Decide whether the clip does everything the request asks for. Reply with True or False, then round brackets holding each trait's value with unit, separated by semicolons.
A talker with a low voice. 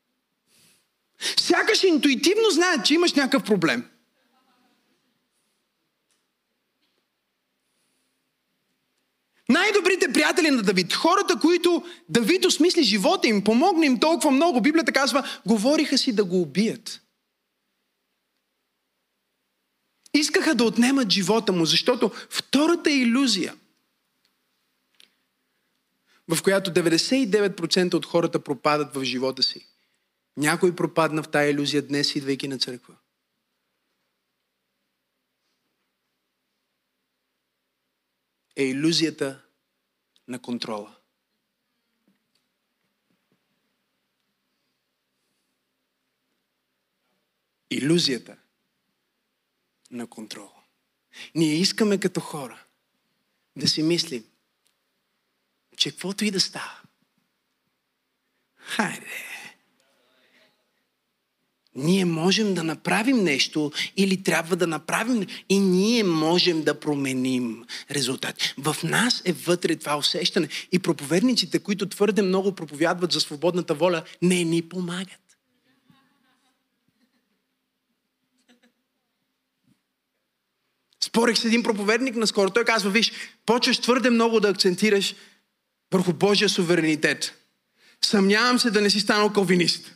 False (185 Hz)